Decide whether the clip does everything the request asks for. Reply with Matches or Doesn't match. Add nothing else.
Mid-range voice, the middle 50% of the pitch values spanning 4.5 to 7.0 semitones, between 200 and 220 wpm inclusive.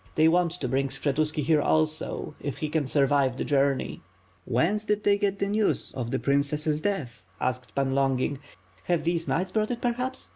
Matches